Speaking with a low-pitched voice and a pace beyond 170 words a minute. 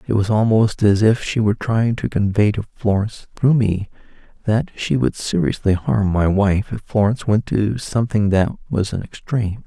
Yes: low, 110 Hz; average, 185 wpm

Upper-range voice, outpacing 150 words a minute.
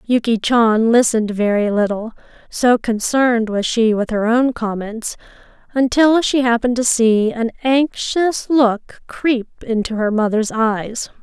No: high, 230 Hz; average, 140 wpm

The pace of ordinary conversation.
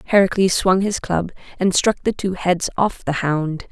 Yes: average, 195 wpm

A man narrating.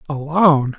Yes: male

